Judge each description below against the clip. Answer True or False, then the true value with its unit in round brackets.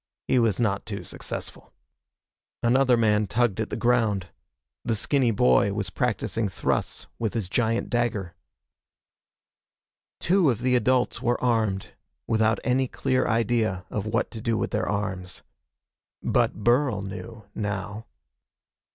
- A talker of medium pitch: False (110 Hz)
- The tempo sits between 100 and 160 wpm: True (135 wpm)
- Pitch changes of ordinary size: True (3.0 semitones)